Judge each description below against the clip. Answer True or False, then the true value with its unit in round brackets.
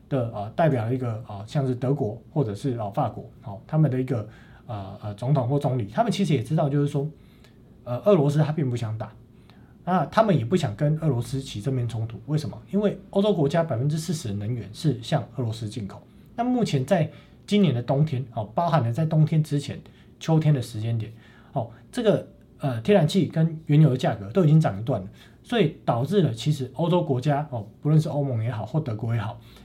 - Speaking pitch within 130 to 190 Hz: True (140 Hz)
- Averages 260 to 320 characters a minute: False (330 characters per minute)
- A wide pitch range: False (5.0 semitones)